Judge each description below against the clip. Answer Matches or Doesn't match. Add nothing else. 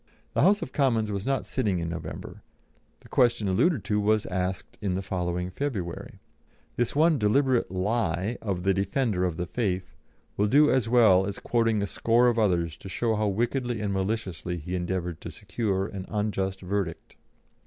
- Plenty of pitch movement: Doesn't match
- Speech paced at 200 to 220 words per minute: Doesn't match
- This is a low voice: Matches